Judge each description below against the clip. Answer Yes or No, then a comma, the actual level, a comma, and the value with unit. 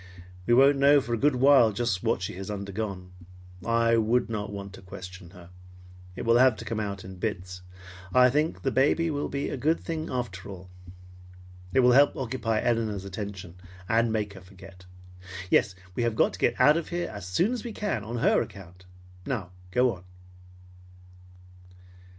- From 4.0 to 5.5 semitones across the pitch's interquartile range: Yes, average, 5.1 semitones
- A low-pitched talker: Yes, low, 110 Hz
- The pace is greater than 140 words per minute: Yes, average, 185 wpm